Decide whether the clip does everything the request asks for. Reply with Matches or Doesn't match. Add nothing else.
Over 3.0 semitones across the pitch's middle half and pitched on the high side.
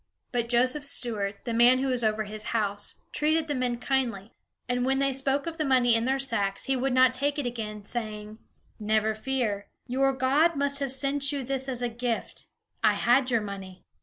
Matches